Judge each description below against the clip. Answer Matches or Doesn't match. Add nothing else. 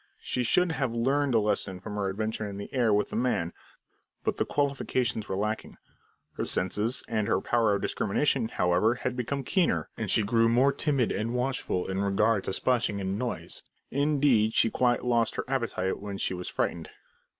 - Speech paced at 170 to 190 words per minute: Matches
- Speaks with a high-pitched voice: Doesn't match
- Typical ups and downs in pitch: Matches